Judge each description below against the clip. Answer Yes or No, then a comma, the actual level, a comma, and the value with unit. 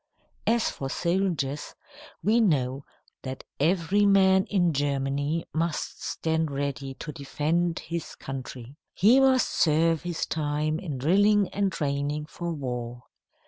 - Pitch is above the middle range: No, medium, 160 Hz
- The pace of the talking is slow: Yes, slow, 125 wpm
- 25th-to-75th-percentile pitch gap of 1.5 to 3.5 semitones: No, average, 4.6 semitones